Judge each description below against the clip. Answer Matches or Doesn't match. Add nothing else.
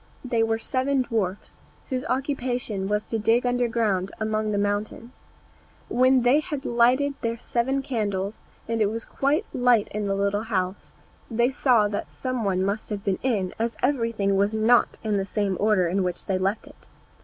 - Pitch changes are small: Doesn't match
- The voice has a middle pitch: Doesn't match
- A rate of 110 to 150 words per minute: Doesn't match